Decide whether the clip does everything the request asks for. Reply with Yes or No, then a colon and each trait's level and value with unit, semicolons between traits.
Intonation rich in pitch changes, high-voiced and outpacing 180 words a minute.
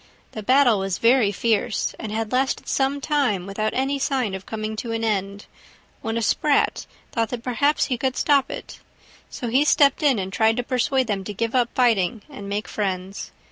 No: average, 4.2 semitones; high, 230 Hz; average, 195 wpm